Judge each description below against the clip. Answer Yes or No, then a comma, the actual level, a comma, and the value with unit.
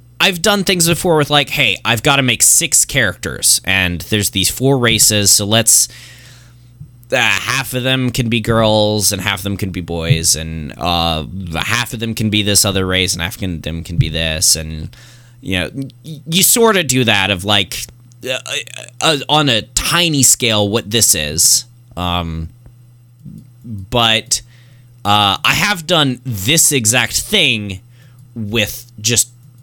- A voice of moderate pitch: No, low, 120 Hz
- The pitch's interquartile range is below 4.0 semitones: No, average, 4.4 semitones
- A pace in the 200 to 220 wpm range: No, average, 165 wpm